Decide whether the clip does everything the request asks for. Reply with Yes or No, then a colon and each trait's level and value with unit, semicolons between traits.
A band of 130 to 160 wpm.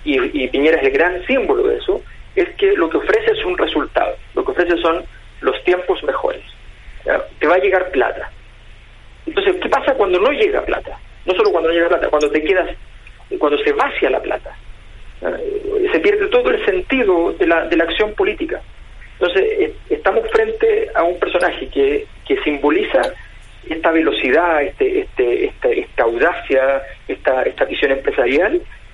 No: average, 170 wpm